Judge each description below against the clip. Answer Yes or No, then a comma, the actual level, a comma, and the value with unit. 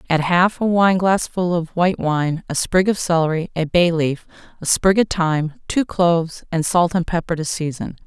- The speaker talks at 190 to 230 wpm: Yes, average, 195 wpm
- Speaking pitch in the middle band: Yes, medium, 170 Hz